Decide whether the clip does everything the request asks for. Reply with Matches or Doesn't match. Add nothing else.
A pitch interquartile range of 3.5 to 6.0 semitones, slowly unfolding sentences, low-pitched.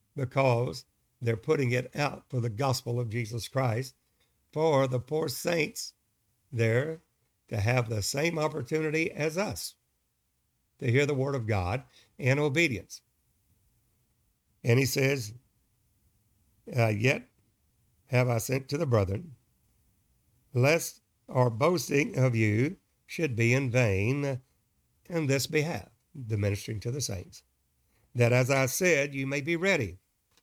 Matches